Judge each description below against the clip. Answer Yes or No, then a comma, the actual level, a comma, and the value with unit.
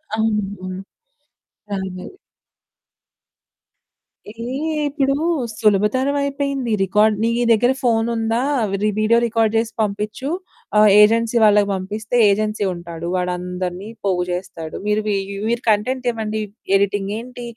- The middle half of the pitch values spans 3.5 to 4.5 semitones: No, average, 2.9 semitones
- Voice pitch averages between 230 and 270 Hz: No, high, 215 Hz